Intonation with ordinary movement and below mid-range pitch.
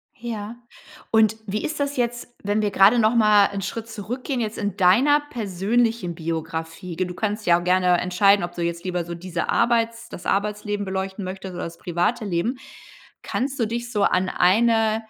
No: average, 4.1 semitones; high, 205 Hz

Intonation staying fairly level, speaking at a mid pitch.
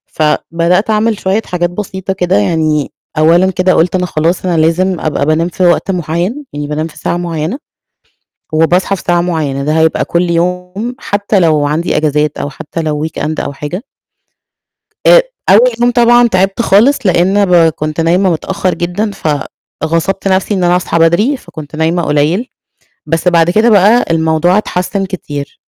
No: average, 3.3 semitones; medium, 175 Hz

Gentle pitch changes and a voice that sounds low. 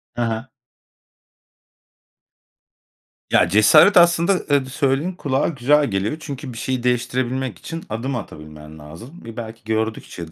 No: average, 4.4 semitones; low, 125 Hz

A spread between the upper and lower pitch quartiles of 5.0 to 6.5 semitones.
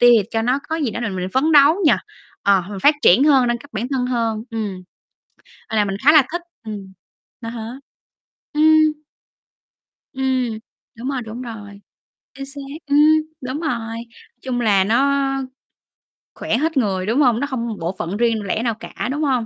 No: average, 4.4 semitones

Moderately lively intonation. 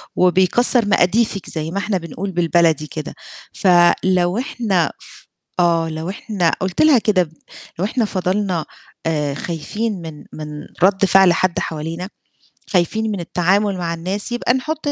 Yes: average, 3.5 semitones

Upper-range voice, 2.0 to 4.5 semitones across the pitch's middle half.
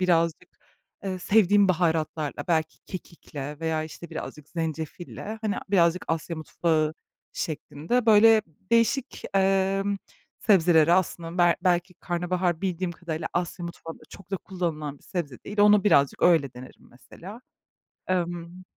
No: medium, 175 Hz; average, 3.1 semitones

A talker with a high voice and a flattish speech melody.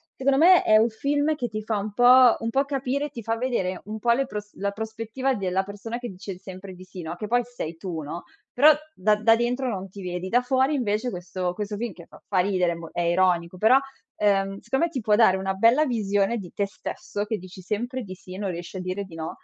No: high, 210 Hz; average, 4.6 semitones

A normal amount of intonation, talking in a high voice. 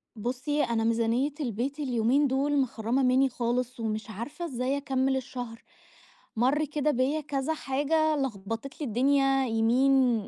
Yes: average, 3.2 semitones; very high, 260 Hz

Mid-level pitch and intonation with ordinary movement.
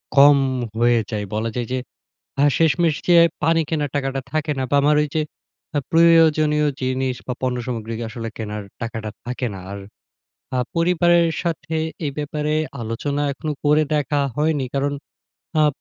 Yes: medium, 145 Hz; average, 4.0 semitones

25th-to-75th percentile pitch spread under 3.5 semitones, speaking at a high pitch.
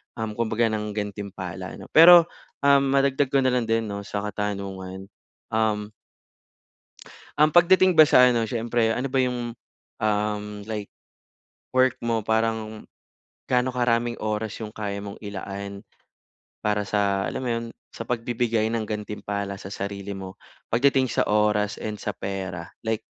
No: average, 2.8 semitones; low, 110 Hz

